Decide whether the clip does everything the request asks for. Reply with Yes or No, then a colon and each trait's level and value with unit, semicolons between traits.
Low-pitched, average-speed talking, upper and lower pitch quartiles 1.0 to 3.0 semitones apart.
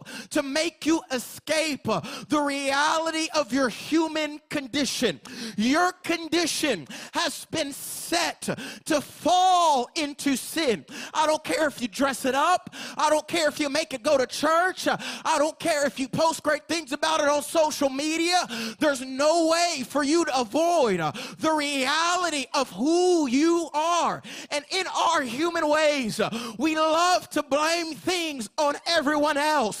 No: very high, 300 Hz; average, 155 wpm; narrow, 2.6 semitones